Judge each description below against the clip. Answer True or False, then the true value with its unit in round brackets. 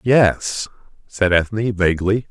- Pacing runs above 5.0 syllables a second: False (3.9 syllables/s)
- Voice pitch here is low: True (100 Hz)